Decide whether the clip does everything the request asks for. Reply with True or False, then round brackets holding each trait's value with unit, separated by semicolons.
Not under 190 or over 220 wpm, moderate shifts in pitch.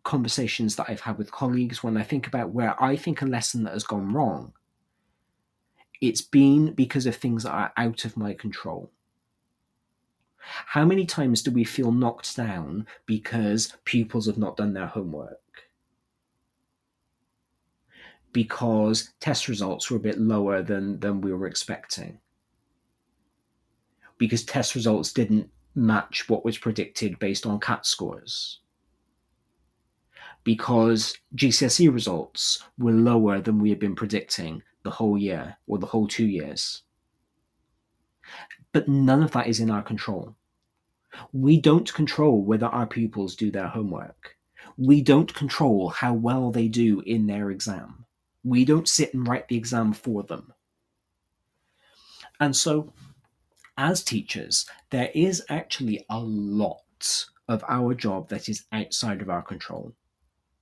False (140 wpm; 3.3 semitones)